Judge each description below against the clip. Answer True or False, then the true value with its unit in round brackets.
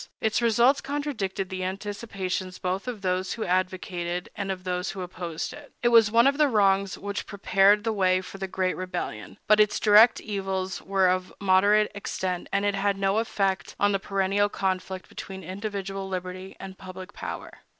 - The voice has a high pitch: True (195 Hz)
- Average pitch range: False (1.9 semitones)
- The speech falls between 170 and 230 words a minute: True (180 wpm)